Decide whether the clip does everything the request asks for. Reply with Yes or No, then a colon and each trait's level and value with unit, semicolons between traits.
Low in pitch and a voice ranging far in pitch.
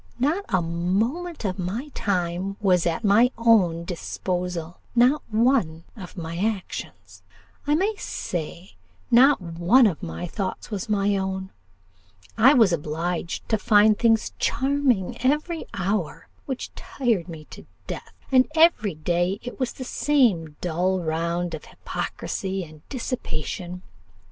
No: high, 195 Hz; wide, 5.8 semitones